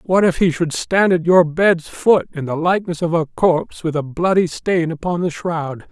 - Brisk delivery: Yes, fast, 225 wpm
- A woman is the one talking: No, male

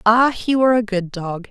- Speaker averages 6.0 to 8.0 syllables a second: No, 5.1 syllables/s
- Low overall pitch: No, high, 220 Hz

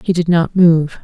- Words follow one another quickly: Yes, fast, 230 wpm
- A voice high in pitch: No, medium, 170 Hz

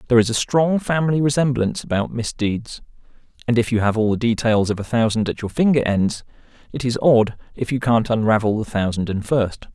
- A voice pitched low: Yes, low, 115 Hz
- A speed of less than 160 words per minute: No, fast, 205 wpm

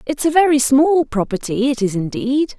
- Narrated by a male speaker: No, female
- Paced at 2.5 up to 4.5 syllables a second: No, 4.9 syllables/s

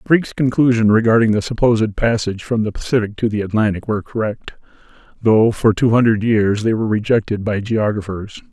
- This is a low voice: Yes, low, 110 Hz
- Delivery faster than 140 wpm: Yes, average, 170 wpm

